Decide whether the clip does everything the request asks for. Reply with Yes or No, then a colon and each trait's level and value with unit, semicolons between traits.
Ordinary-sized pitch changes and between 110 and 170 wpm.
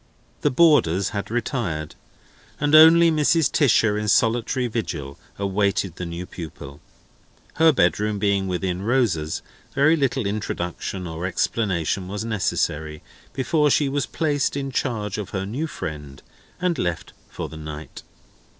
No: wide, 7.5 semitones; slow, 135 wpm